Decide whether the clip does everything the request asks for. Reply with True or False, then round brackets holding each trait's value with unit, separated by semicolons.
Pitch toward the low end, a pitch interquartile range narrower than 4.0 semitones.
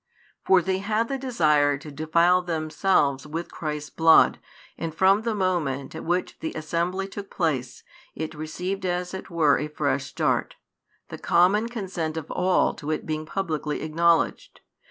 False (165 Hz; 3.5 semitones)